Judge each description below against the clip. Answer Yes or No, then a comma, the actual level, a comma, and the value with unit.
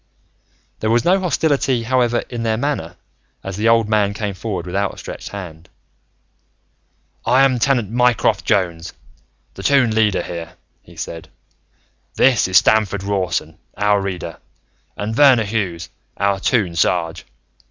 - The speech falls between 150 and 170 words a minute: No, slow, 135 wpm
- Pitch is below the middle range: Yes, low, 105 Hz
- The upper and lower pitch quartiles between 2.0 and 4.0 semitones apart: No, average, 4.6 semitones